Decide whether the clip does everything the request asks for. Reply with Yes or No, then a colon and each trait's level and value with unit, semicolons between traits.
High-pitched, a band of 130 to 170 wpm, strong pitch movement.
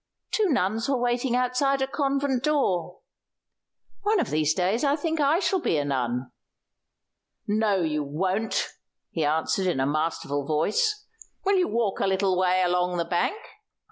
Yes: high, 200 Hz; average, 160 wpm; wide, 8.9 semitones